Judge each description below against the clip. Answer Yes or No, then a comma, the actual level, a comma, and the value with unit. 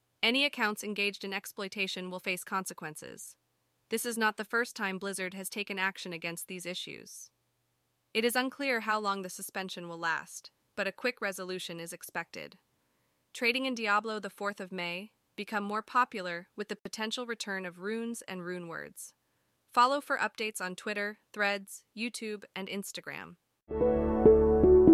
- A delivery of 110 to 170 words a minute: Yes, average, 155 wpm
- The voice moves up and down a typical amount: Yes, average, 3.1 semitones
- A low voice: No, high, 200 Hz